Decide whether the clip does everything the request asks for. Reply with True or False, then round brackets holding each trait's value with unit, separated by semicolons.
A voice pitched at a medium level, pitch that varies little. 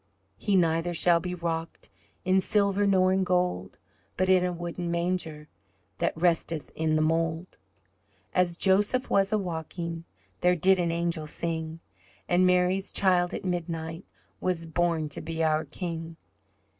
True (175 Hz; 2.1 semitones)